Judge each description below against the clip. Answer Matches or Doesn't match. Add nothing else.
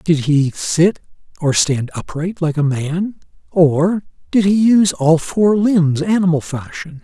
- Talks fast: Doesn't match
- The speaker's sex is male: Matches